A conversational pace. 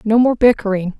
Yes: average, 180 wpm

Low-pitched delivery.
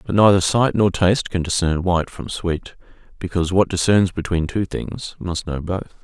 Yes: very low, 90 Hz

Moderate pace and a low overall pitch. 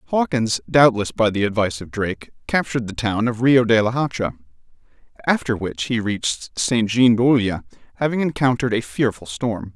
Yes: average, 165 wpm; low, 115 Hz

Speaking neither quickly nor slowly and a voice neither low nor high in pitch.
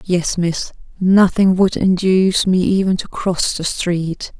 Yes: average, 150 wpm; medium, 180 Hz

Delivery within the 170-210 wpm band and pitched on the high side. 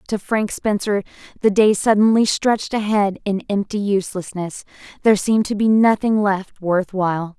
No: average, 145 wpm; high, 205 Hz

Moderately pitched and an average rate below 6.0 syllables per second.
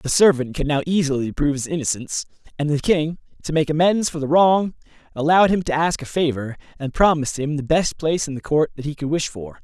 No: medium, 150 Hz; 6.1 syllables/s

